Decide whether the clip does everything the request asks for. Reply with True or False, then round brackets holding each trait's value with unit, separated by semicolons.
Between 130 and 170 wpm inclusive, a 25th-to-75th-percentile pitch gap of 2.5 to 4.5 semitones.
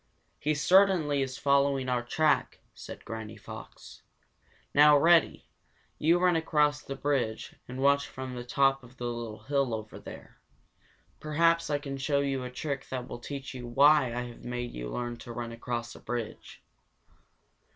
True (165 wpm; 3.3 semitones)